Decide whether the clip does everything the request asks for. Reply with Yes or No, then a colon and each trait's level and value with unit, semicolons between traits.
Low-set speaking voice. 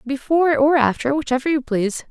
No: very high, 275 Hz